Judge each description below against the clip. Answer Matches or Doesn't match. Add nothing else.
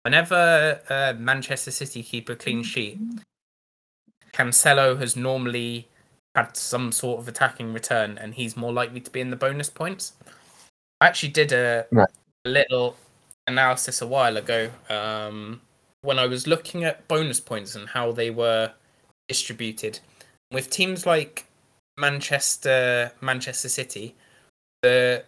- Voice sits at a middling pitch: Doesn't match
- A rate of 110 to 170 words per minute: Matches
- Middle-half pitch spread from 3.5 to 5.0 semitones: Doesn't match